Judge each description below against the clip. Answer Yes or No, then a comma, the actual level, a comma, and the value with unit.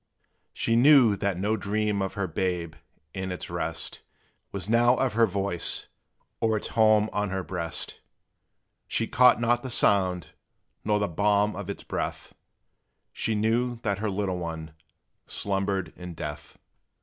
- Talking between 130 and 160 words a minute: Yes, average, 150 wpm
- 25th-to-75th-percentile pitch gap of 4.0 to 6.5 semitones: No, average, 3.0 semitones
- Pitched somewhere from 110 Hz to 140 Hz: No, low, 100 Hz